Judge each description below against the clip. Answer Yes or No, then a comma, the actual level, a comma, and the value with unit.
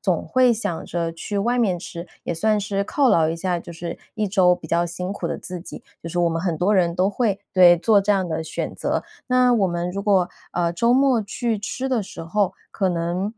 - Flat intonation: No, average, 3.6 semitones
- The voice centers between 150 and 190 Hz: Yes, medium, 185 Hz